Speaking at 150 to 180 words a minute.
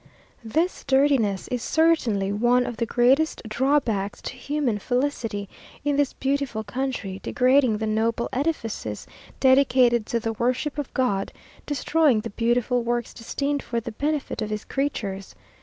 No: average, 140 wpm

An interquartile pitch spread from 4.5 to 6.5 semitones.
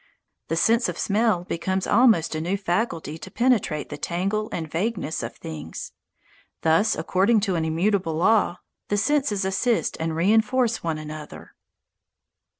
Yes: average, 5.3 semitones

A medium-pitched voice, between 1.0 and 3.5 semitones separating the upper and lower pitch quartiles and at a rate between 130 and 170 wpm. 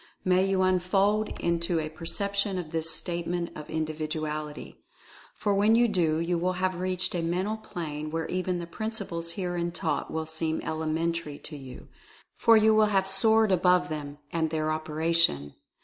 Yes: medium, 170 Hz; average, 3.0 semitones; average, 165 wpm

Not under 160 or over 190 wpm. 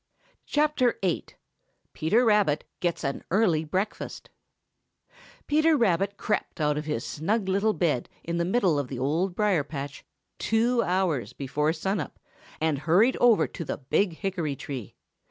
No: average, 145 wpm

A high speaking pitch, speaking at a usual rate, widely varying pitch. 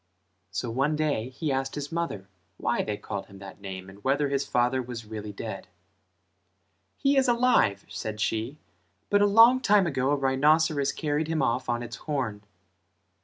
No: low, 135 Hz; average, 170 wpm; wide, 6.0 semitones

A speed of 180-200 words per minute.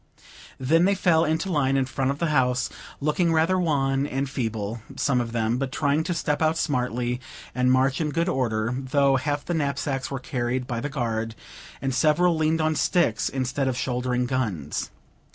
Yes: average, 185 wpm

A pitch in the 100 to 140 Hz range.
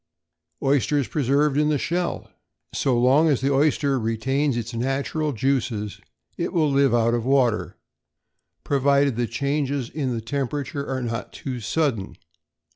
Yes: low, 135 Hz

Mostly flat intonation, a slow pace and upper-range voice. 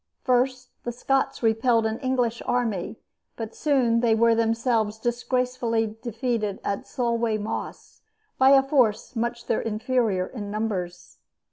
Yes: narrow, 2.2 semitones; slow, 130 wpm; high, 230 Hz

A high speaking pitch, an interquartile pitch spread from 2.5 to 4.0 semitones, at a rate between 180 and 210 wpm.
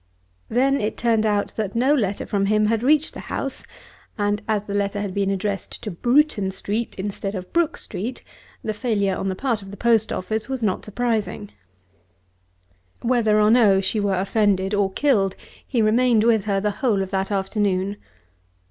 Yes: high, 210 Hz; average, 2.8 semitones; average, 185 wpm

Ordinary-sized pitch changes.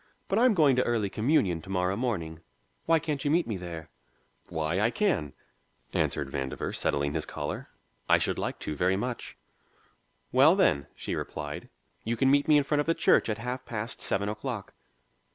No: wide, 8.5 semitones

